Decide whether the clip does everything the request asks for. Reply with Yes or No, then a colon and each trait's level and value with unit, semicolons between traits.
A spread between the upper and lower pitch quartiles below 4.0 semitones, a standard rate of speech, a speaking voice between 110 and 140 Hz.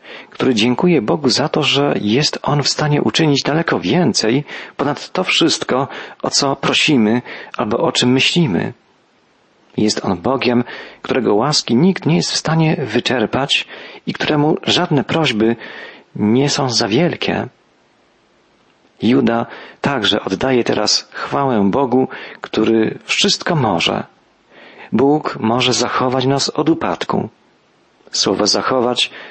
No: average, 4.4 semitones; average, 120 wpm; low, 130 Hz